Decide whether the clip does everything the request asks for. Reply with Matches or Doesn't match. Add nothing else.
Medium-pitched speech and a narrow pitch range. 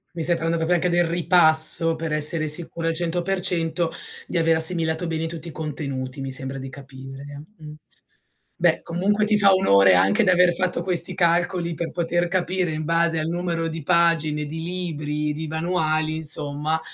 Matches